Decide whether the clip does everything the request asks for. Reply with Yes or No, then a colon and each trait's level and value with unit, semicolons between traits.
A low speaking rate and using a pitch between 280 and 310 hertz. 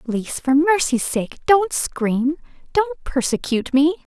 Yes: slow, 130 wpm; very high, 290 Hz